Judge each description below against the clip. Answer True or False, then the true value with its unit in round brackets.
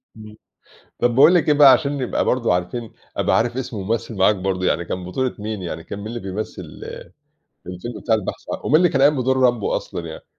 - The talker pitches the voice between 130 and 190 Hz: False (115 Hz)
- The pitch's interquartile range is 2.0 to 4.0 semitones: False (5.4 semitones)